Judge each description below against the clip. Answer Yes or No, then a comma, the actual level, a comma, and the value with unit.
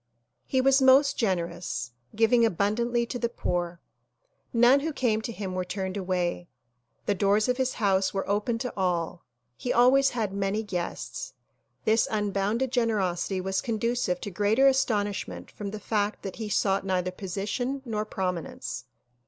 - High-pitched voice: Yes, high, 210 Hz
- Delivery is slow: No, average, 155 wpm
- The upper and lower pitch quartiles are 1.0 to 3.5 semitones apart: No, average, 4.1 semitones